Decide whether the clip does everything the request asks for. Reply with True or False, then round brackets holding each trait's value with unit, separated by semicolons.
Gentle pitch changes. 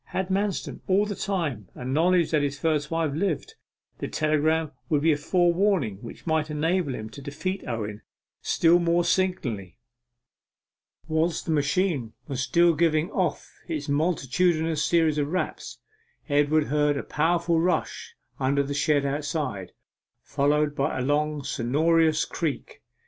False (3.1 semitones)